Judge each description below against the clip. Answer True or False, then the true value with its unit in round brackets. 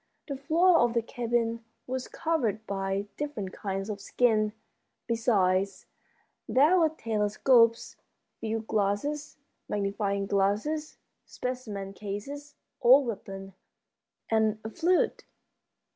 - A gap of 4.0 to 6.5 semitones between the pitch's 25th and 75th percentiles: True (5.0 semitones)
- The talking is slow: True (100 wpm)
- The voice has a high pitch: True (225 Hz)